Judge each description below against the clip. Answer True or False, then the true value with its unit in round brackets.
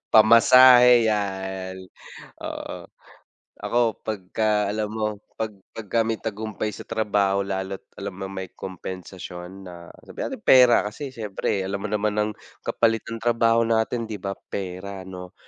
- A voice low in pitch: True (105 Hz)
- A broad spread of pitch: False (2.9 semitones)